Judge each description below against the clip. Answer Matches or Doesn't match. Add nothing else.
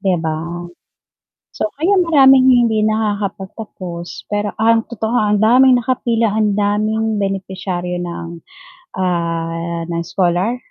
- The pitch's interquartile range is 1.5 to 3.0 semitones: Doesn't match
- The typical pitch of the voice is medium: Doesn't match